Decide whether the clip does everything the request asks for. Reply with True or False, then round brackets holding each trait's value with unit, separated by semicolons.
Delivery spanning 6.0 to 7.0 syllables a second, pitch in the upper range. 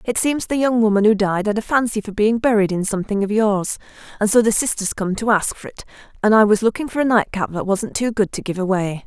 True (6.1 syllables/s; 210 Hz)